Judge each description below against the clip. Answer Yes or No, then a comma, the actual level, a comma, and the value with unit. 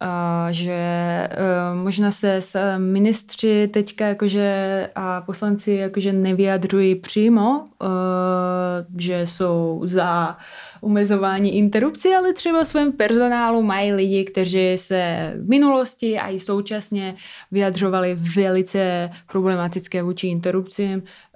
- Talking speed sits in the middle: No, slow, 110 wpm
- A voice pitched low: No, high, 195 Hz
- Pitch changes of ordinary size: No, narrow, 2.3 semitones